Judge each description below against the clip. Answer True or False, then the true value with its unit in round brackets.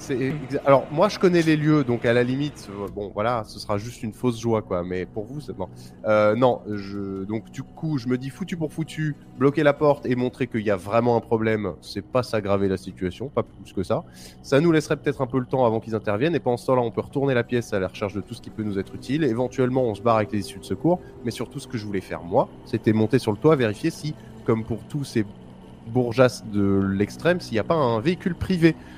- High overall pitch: False (120 Hz)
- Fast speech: True (265 wpm)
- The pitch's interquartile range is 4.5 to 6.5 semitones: True (4.8 semitones)